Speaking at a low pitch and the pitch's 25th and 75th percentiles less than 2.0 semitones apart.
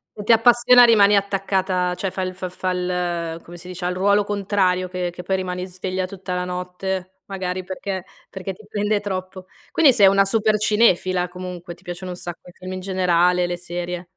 No: medium, 185 Hz; narrow, 1.6 semitones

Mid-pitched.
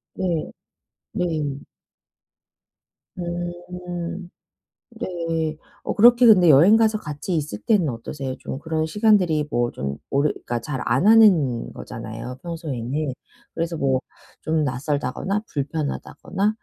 Yes: medium, 160 Hz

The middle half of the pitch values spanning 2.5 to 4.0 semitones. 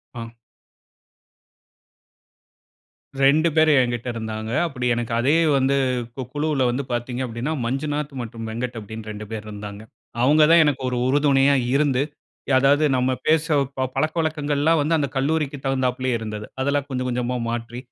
Yes: average, 3.5 semitones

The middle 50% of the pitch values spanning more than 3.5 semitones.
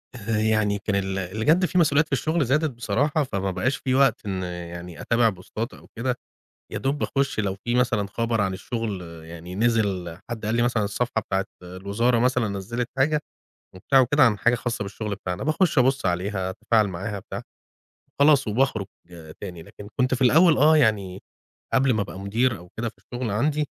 Yes: average, 4.9 semitones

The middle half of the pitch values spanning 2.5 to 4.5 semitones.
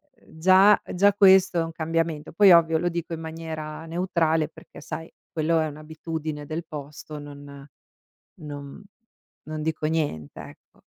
No: narrow, 1.7 semitones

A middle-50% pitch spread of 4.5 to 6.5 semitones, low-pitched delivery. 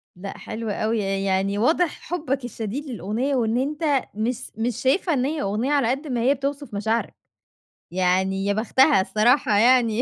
No: average, 5.0 semitones; high, 235 Hz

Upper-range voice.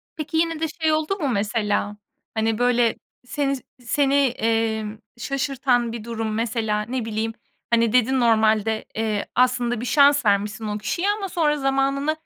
Yes: high, 240 Hz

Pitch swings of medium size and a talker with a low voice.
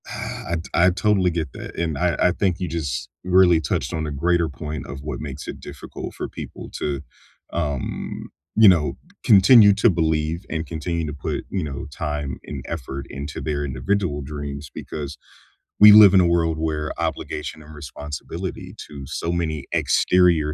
Yes: average, 3.2 semitones; very low, 80 Hz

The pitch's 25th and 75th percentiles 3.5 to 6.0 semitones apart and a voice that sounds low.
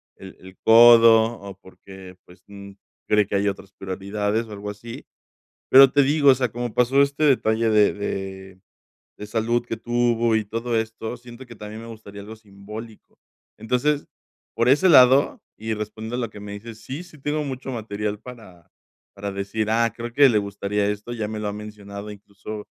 No: average, 2.8 semitones; low, 110 Hz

